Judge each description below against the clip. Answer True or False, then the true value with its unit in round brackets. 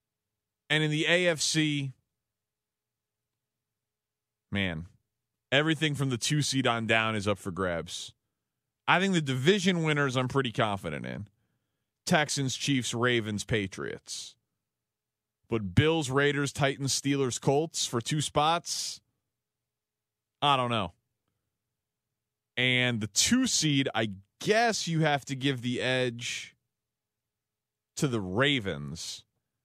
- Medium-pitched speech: False (120 Hz)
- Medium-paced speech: False (115 wpm)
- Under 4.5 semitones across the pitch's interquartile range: False (4.8 semitones)